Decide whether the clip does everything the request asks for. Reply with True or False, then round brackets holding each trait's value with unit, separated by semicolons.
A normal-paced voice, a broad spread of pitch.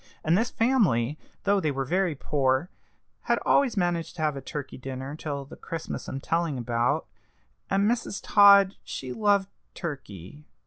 True (160 wpm; 6.5 semitones)